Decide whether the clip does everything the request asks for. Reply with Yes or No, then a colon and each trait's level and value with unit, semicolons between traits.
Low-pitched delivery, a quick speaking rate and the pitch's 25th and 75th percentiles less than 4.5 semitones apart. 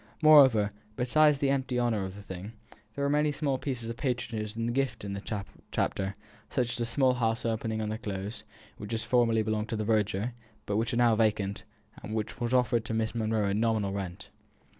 Yes: low, 115 Hz; fast, 215 wpm; narrow, 2.6 semitones